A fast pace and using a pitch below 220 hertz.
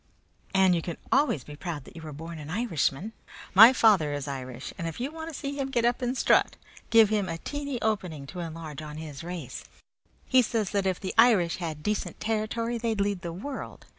Yes: fast, 215 wpm; high, 190 Hz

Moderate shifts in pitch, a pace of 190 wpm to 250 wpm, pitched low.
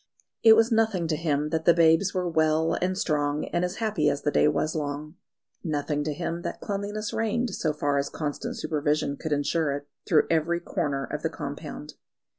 No: average, 3.3 semitones; average, 195 wpm; medium, 160 Hz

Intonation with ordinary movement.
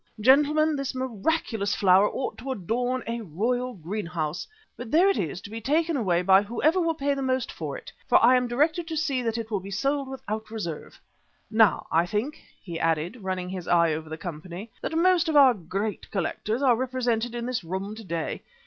No: wide, 6.0 semitones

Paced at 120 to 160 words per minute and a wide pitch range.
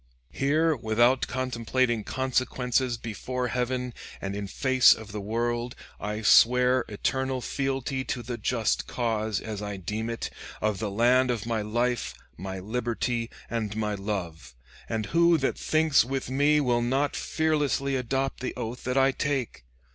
No: average, 150 wpm; average, 3.2 semitones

